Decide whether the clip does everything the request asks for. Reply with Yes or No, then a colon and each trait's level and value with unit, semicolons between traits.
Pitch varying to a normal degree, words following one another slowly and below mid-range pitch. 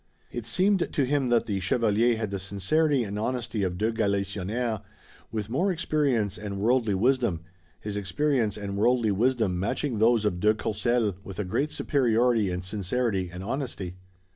No: average, 3.9 semitones; average, 165 wpm; low, 110 Hz